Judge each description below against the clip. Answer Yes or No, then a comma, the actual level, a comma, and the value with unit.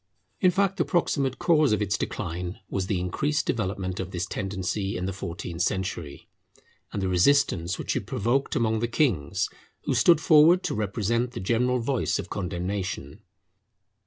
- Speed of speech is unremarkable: Yes, average, 160 wpm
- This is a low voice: Yes, low, 100 Hz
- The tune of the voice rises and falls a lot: Yes, wide, 6.0 semitones